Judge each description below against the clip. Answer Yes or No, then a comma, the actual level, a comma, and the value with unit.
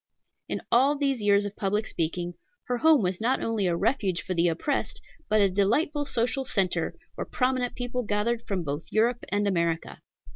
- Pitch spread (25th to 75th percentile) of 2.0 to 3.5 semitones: No, average, 5.1 semitones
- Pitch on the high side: Yes, high, 210 Hz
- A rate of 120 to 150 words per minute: No, average, 180 wpm